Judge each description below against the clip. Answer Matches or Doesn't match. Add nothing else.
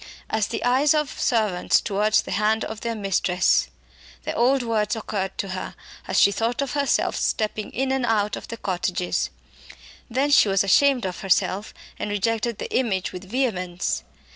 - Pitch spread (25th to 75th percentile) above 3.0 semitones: Matches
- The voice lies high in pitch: Matches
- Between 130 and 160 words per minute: Doesn't match